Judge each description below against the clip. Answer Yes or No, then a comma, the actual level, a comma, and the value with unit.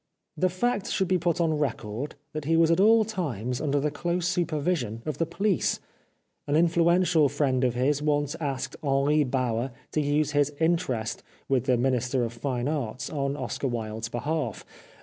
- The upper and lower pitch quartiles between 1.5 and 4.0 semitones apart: No, average, 4.6 semitones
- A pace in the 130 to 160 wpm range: No, average, 170 wpm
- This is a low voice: No, medium, 145 Hz